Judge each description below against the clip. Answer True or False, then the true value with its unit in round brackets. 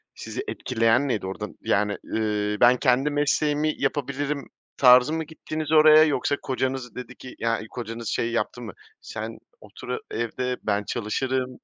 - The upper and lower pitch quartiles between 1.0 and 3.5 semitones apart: False (4.1 semitones)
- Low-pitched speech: True (125 Hz)